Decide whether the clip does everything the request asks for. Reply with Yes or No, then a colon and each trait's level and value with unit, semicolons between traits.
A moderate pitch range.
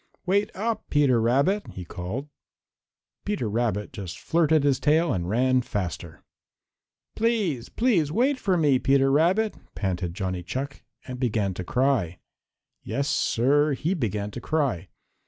No: wide, 7.6 semitones